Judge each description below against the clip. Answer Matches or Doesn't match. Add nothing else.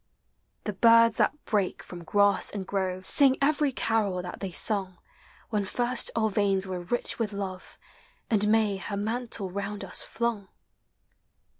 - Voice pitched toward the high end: Matches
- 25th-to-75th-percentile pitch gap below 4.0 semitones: Matches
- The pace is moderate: Matches